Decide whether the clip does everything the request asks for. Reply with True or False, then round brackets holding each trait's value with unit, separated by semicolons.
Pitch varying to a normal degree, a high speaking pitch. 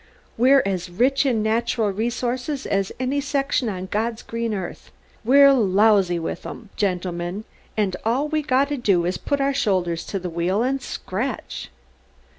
False (5.9 semitones; 220 Hz)